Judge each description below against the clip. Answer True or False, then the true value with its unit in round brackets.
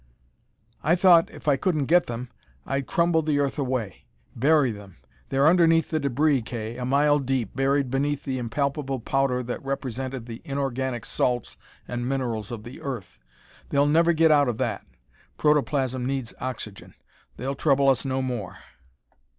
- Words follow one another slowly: False (160 wpm)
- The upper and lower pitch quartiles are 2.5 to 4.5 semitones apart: True (3.0 semitones)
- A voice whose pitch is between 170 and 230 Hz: False (135 Hz)